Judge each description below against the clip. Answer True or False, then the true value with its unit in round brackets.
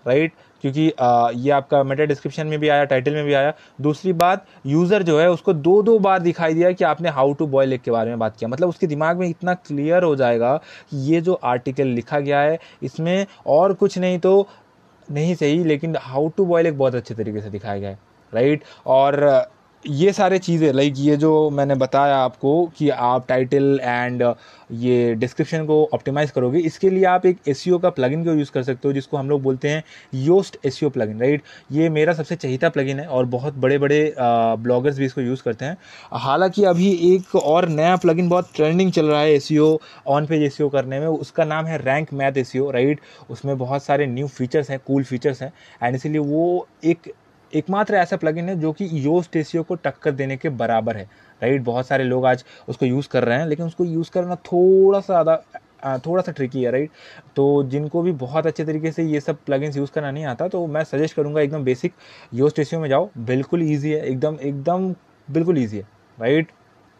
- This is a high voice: False (150 Hz)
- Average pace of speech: False (210 wpm)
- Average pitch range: True (3.9 semitones)